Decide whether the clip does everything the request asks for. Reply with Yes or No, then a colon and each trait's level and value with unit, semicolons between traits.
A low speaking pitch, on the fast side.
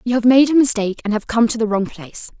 No: high, 225 Hz; fast, 300 wpm